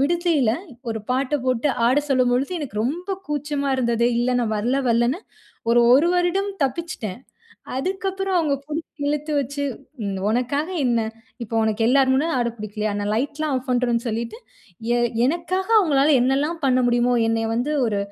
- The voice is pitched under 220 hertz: No, very high, 265 Hz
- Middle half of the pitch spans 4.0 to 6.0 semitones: Yes, average, 4.4 semitones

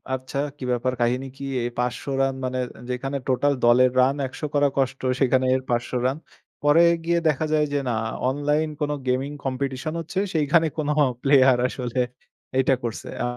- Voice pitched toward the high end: No, low, 135 Hz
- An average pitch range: No, narrow, 2.2 semitones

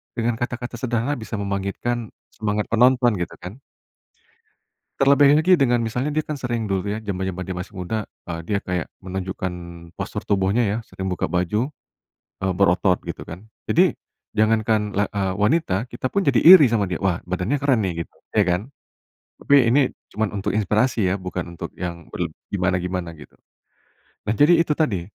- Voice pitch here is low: Yes, low, 105 Hz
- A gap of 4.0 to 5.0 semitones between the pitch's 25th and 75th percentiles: Yes, average, 4.7 semitones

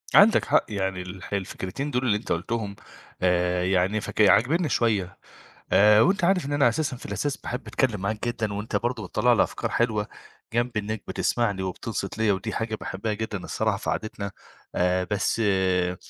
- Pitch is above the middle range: No, low, 105 Hz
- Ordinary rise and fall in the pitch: Yes, average, 3.7 semitones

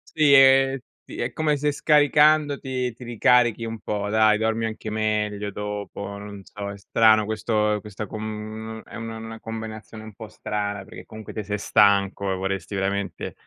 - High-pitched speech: No, low, 110 Hz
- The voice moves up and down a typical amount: No, narrow, 2.0 semitones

